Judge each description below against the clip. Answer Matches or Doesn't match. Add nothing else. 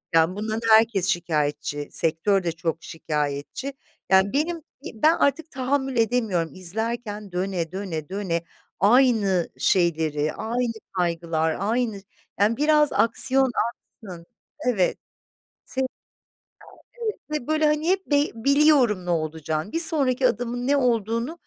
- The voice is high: Matches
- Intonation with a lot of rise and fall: Matches